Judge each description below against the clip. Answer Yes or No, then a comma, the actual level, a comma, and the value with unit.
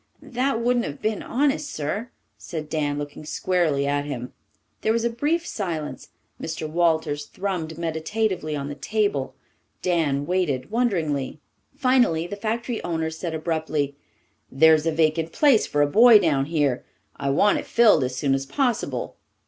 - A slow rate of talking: No, average, 155 wpm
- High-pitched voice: No, medium, 160 Hz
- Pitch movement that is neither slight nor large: No, wide, 6.9 semitones